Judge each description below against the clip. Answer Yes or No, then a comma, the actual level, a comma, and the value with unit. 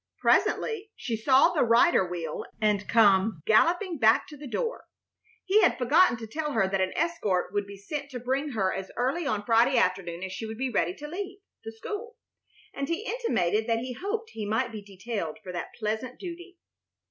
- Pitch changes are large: Yes, wide, 8.1 semitones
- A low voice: No, high, 235 Hz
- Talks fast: No, average, 195 wpm